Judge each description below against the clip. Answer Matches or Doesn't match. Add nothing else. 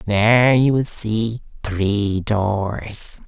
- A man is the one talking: Matches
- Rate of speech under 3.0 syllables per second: Matches